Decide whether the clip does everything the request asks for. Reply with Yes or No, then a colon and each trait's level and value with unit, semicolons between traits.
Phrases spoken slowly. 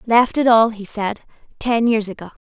No: average, 200 wpm